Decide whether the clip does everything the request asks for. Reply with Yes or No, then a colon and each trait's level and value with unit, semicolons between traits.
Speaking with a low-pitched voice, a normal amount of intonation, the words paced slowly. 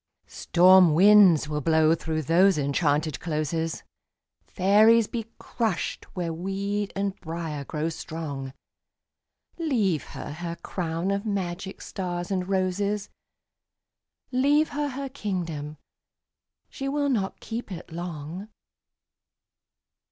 No: medium, 180 Hz; average, 4.2 semitones; slow, 105 wpm